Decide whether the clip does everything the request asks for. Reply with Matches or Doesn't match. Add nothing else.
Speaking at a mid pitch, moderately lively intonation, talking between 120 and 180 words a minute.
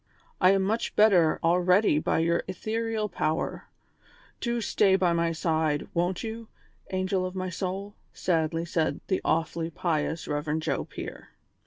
Matches